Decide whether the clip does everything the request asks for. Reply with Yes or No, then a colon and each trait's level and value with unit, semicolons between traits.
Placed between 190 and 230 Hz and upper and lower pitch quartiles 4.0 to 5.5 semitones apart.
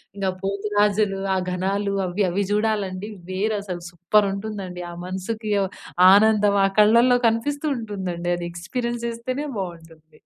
No: high, 200 Hz; average, 2.8 semitones